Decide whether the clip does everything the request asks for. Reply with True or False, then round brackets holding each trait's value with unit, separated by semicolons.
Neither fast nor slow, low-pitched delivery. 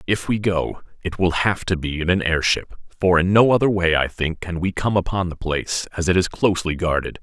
False (240 wpm; 90 Hz)